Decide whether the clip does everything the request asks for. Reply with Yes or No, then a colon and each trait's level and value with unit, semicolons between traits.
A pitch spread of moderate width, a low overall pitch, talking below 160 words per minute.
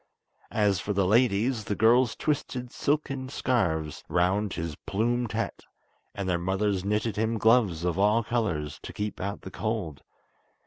Yes: average, 3.9 semitones; low, 105 Hz; average, 150 wpm